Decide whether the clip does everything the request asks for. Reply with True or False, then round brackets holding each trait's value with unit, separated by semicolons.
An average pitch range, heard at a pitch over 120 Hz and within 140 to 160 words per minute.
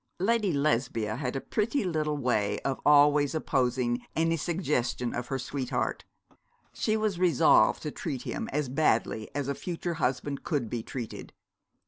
True (4.8 semitones; 140 Hz; 150 wpm)